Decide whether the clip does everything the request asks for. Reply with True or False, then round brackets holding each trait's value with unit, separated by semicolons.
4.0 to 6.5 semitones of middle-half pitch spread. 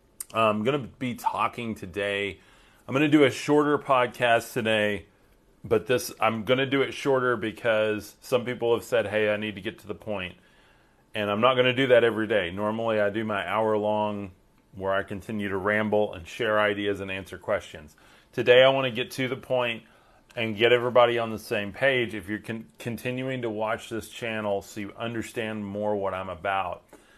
False (3.1 semitones)